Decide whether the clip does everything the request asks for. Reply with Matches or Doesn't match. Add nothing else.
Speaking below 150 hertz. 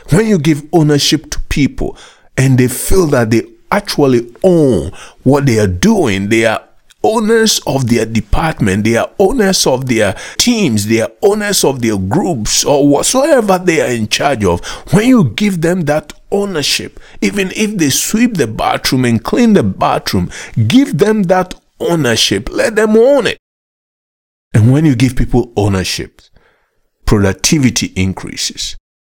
Matches